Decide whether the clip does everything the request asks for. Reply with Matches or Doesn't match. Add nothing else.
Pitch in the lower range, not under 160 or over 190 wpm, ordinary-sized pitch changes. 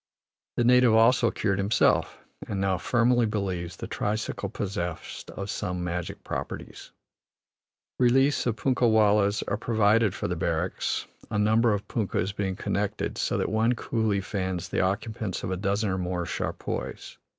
Doesn't match